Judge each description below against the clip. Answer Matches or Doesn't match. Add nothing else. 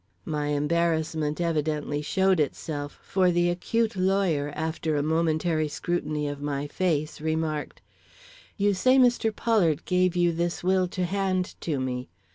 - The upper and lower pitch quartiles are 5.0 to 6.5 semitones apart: Doesn't match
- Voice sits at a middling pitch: Matches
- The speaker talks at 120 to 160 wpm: Matches